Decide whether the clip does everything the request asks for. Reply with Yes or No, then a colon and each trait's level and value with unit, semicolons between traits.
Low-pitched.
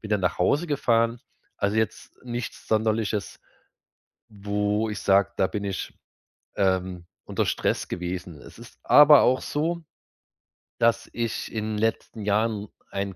Yes: low, 105 Hz